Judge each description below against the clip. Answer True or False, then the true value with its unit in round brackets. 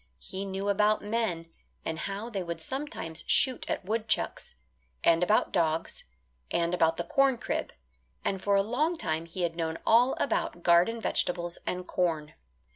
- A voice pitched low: False (185 Hz)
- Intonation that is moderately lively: True (4.8 semitones)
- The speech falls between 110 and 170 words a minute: True (160 wpm)